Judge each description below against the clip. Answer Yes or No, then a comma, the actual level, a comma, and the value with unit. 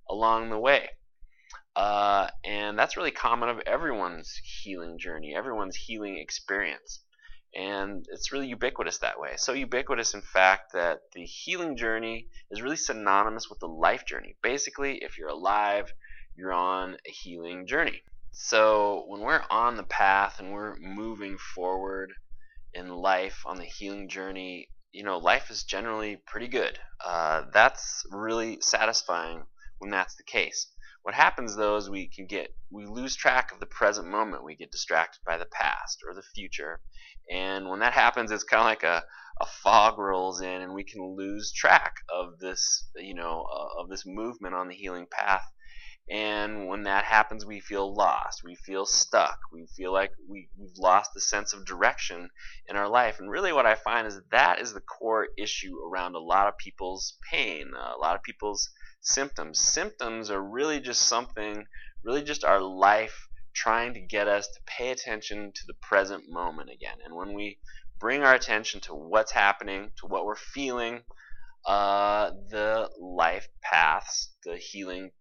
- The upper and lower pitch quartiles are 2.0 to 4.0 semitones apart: Yes, narrow, 2.6 semitones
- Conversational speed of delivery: Yes, average, 170 wpm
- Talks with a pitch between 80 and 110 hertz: Yes, low, 100 Hz